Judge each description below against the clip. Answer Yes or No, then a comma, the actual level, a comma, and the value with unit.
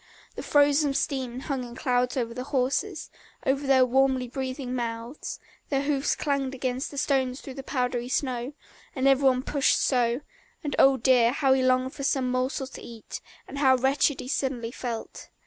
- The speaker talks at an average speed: Yes, average, 180 wpm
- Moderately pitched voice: No, very high, 260 Hz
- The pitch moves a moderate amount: No, narrow, 1.7 semitones